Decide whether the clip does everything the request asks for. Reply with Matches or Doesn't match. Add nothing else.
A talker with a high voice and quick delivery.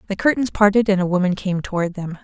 Matches